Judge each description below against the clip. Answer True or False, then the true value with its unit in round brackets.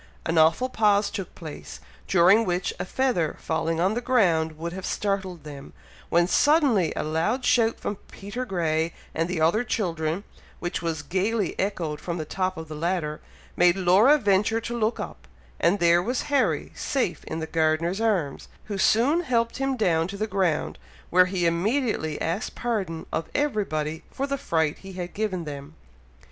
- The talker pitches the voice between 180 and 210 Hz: True (185 Hz)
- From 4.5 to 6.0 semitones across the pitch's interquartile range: True (5.2 semitones)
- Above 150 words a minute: True (175 wpm)